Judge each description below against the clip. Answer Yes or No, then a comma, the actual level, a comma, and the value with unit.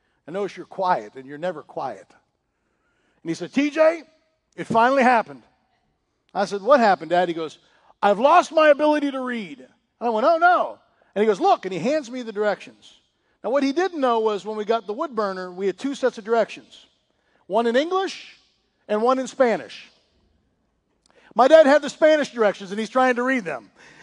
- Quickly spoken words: No, average, 195 wpm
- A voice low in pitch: No, high, 235 Hz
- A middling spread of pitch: No, wide, 6.5 semitones